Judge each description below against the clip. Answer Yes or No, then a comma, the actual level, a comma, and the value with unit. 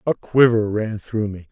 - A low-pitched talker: Yes, low, 110 Hz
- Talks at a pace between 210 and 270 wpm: No, average, 200 wpm